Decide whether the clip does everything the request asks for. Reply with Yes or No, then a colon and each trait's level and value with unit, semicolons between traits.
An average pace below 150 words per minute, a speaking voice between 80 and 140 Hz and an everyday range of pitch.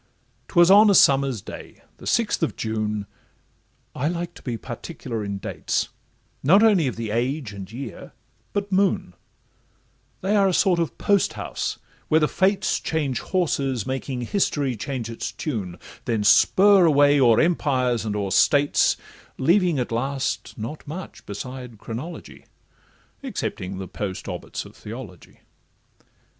No: average, 140 wpm; low, 135 Hz; wide, 7.2 semitones